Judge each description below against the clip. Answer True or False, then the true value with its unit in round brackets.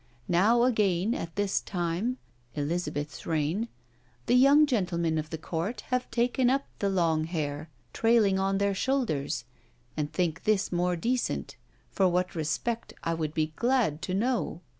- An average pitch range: False (6.4 semitones)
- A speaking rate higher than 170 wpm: False (150 wpm)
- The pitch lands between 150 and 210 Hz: True (185 Hz)